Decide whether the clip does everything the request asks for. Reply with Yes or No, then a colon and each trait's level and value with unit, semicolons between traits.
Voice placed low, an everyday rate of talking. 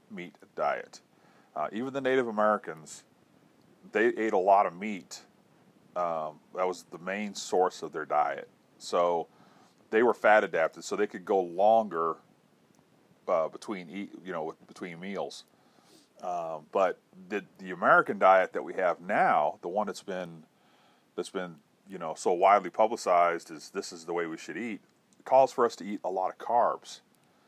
Yes: very low, 95 Hz; average, 170 wpm